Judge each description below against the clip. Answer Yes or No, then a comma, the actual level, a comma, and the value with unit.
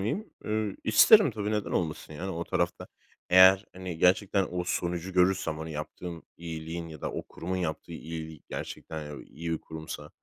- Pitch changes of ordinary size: Yes, average, 3.1 semitones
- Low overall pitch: Yes, very low, 85 Hz